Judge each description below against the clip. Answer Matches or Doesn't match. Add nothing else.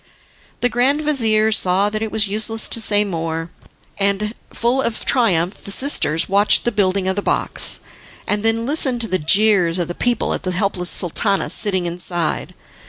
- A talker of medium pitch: Doesn't match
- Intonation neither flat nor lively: Matches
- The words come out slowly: Doesn't match